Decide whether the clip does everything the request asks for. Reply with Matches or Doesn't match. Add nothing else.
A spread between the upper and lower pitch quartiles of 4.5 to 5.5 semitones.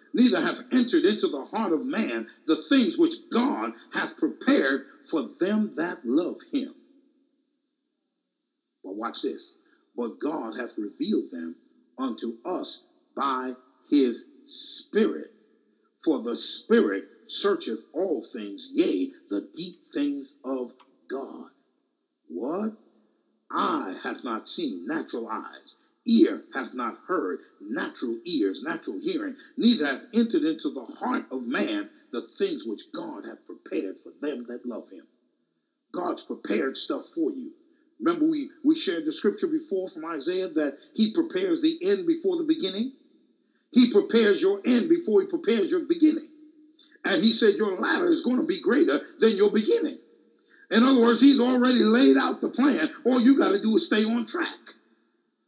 Matches